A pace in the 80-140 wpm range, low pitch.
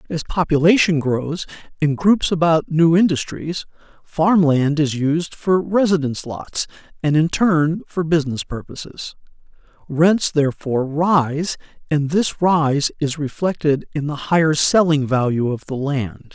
No: slow, 135 wpm; medium, 155 Hz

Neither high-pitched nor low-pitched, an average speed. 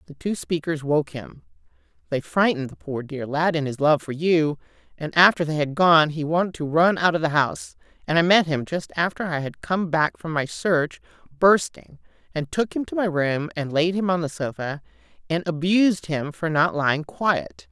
No: medium, 160 Hz; fast, 210 wpm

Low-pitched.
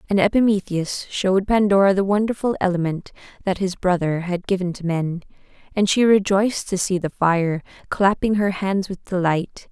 No: high, 190 Hz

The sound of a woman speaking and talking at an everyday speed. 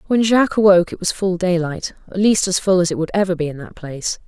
No: female; fast, 255 wpm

